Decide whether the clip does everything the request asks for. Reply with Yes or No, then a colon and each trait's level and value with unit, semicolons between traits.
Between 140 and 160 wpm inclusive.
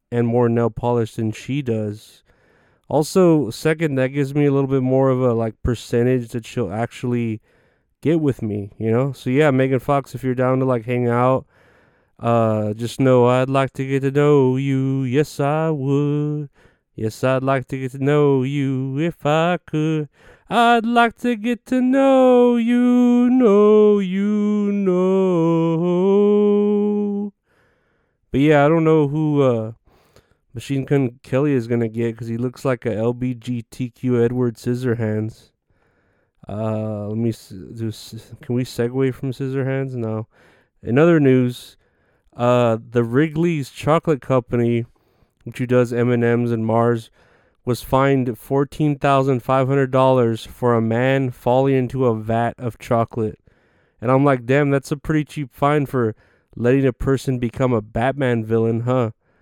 Yes: average, 155 wpm